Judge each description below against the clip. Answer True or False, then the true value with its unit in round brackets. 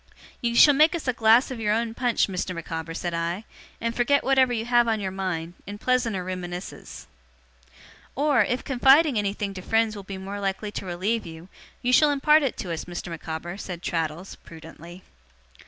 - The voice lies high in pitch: True (205 Hz)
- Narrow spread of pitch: False (5.5 semitones)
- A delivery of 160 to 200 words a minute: True (190 wpm)